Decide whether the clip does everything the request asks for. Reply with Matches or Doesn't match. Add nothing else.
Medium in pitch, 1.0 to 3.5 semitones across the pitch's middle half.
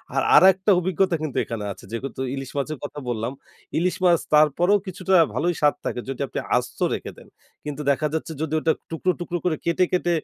Doesn't match